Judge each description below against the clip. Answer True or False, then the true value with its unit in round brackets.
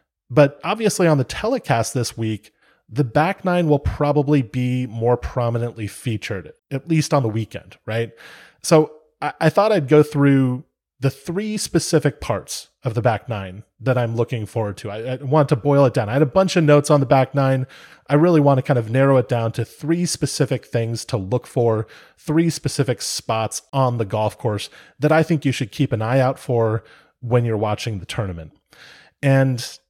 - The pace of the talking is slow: False (195 wpm)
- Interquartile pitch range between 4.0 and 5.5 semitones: True (4.4 semitones)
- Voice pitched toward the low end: True (130 Hz)